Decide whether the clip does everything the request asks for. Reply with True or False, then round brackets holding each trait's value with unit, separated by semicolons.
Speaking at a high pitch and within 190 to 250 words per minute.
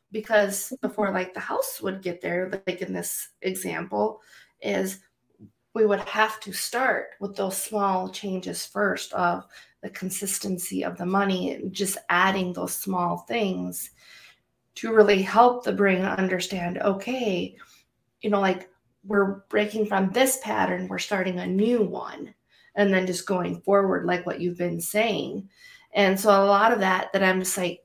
False (195 Hz; 160 wpm)